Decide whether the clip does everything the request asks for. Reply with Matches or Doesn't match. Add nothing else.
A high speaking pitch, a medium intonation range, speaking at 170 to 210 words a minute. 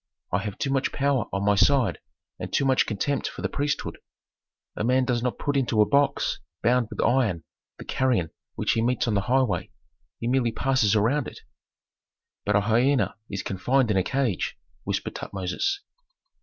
Doesn't match